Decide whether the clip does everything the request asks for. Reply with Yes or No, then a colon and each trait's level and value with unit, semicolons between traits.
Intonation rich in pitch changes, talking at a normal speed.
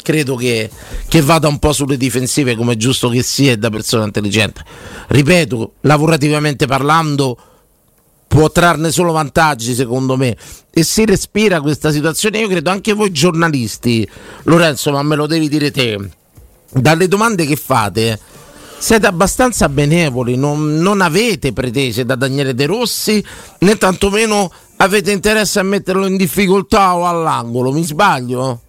Yes: wide, 6.2 semitones; average, 140 wpm